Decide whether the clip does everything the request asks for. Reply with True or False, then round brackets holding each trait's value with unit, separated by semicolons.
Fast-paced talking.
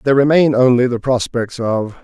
False (175 wpm)